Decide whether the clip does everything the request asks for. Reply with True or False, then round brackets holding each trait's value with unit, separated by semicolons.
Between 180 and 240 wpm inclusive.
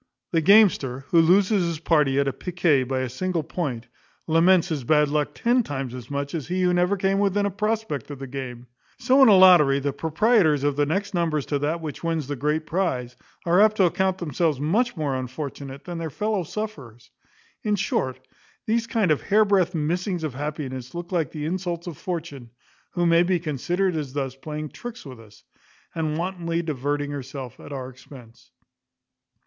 True (185 wpm)